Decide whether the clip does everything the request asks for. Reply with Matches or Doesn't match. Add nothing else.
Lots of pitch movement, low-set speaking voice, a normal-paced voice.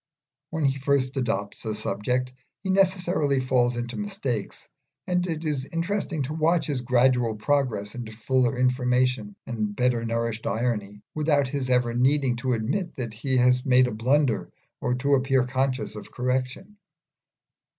Doesn't match